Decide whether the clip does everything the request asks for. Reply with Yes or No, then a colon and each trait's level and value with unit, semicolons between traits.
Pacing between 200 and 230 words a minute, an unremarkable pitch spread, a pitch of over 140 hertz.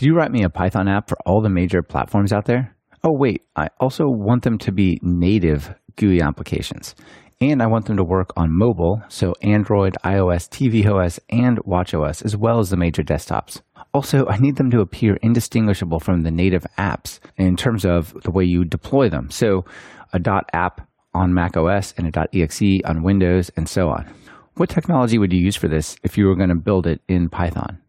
No: fast, 205 wpm; average, 4.1 semitones; very low, 95 Hz